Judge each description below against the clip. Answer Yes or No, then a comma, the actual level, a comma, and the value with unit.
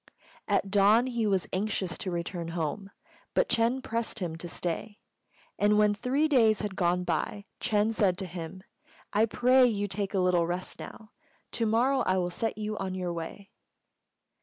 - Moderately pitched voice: No, high, 205 Hz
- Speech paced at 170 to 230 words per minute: Yes, average, 175 wpm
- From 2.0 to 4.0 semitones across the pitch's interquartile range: Yes, average, 3.7 semitones